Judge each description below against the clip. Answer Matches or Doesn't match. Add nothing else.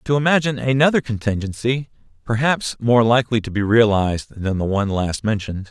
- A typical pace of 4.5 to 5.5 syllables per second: Doesn't match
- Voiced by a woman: Doesn't match